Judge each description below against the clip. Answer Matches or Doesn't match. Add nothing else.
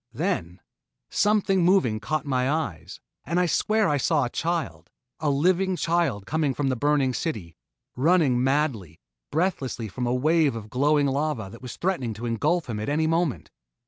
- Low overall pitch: Doesn't match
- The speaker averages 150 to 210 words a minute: Matches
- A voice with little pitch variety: Doesn't match